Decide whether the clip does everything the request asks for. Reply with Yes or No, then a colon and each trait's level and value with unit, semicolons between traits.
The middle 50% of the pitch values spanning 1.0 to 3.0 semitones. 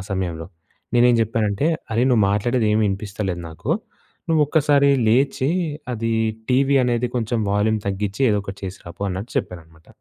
No: average, 4.2 semitones